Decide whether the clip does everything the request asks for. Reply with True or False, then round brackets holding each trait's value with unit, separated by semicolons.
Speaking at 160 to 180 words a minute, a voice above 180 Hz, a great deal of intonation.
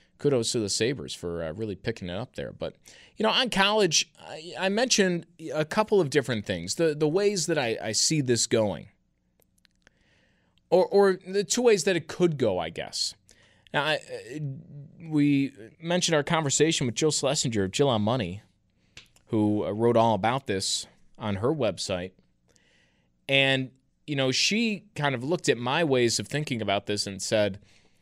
False (175 wpm; 140 Hz; 8.0 semitones)